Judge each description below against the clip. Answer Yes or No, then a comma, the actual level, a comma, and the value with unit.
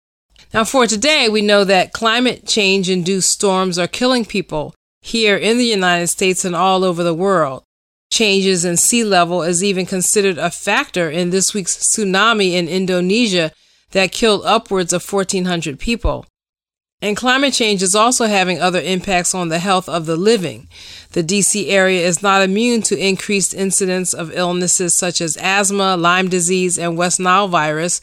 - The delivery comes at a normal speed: Yes, average, 165 wpm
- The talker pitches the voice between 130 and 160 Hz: No, high, 190 Hz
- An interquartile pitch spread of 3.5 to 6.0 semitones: No, narrow, 2.6 semitones